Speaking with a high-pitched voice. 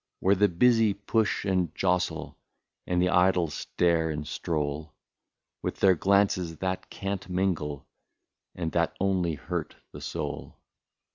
No: very low, 90 Hz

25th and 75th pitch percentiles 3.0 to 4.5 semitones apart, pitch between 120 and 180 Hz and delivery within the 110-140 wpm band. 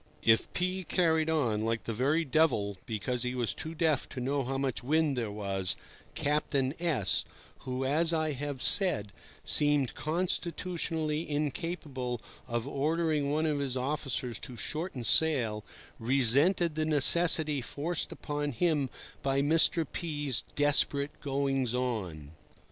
Yes: average, 4.1 semitones; medium, 140 Hz; slow, 135 wpm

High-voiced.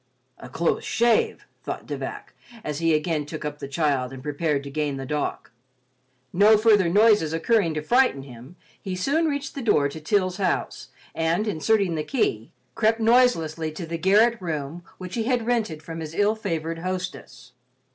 No: medium, 170 Hz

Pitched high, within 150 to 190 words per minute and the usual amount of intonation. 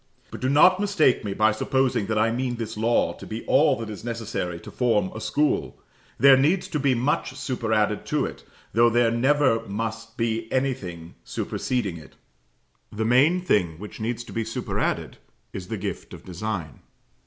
No: low, 115 Hz; average, 175 wpm; average, 3.5 semitones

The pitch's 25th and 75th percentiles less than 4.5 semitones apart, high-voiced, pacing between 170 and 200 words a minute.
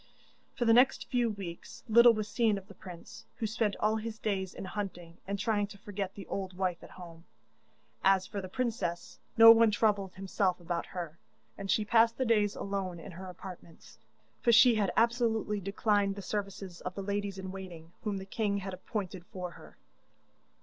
Yes: average, 2.7 semitones; high, 200 Hz; average, 190 wpm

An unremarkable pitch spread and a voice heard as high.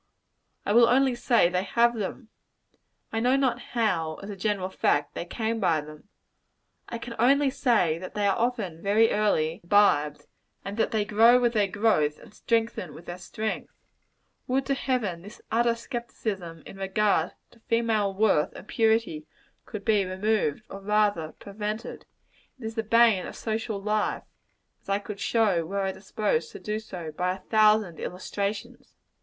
Yes: average, 3.5 semitones; high, 210 Hz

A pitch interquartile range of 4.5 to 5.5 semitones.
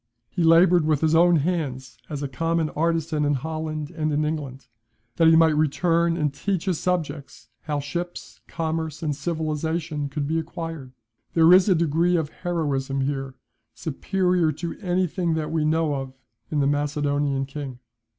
No: narrow, 2.5 semitones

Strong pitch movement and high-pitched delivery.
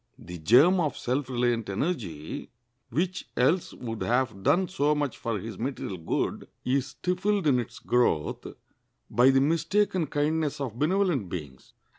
No: wide, 6.1 semitones; low, 135 Hz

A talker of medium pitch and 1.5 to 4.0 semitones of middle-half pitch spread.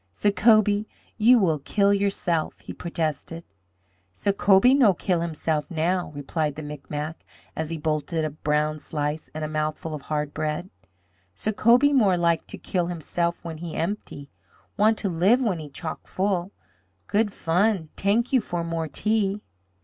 No: medium, 170 Hz; average, 4.6 semitones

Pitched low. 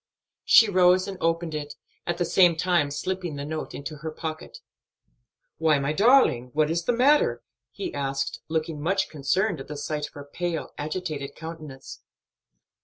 No: medium, 160 Hz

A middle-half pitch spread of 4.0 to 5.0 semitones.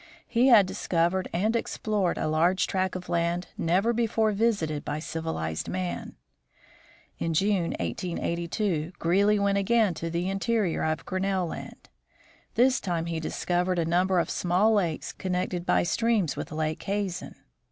No: average, 3.4 semitones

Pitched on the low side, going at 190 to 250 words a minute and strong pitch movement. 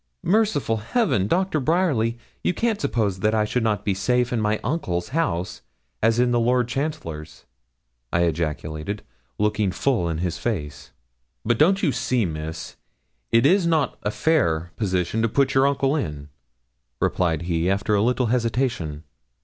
No: low, 110 Hz; average, 160 wpm; wide, 7.4 semitones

